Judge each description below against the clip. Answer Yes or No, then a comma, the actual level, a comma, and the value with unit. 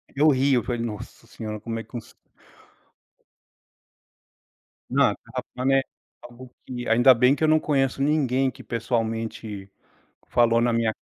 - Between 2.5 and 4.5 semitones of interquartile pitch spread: Yes, average, 2.8 semitones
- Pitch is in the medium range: No, low, 120 Hz